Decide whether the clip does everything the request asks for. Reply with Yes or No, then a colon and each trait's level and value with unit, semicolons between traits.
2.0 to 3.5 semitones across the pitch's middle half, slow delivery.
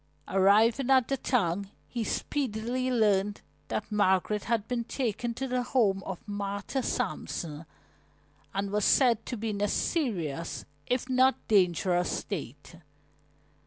No: average, 4.2 semitones; slow, 130 wpm